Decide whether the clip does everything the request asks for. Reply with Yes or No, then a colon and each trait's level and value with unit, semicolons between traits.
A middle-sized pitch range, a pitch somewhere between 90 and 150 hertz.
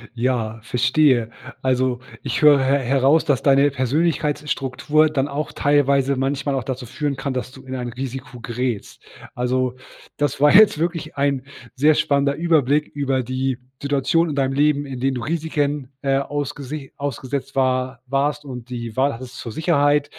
No: narrow, 2.1 semitones; low, 135 Hz